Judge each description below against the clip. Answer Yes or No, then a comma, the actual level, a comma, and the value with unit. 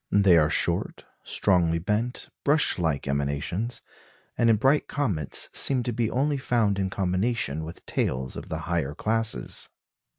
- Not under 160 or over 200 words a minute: No, average, 145 wpm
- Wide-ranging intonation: Yes, wide, 6.8 semitones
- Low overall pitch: Yes, low, 100 Hz